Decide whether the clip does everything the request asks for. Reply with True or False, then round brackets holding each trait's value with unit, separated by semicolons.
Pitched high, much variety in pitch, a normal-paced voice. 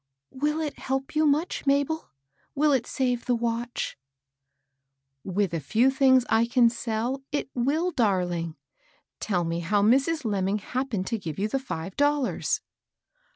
True (235 Hz; 6.3 semitones; 155 wpm)